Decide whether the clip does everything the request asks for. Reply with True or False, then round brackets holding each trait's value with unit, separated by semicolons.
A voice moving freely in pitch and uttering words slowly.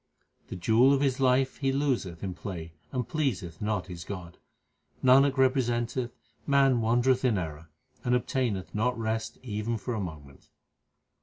False (5.7 semitones; 155 wpm)